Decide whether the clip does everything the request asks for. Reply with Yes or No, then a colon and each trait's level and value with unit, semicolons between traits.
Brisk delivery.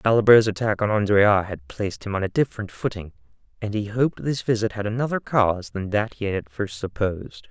Yes: fast, 210 wpm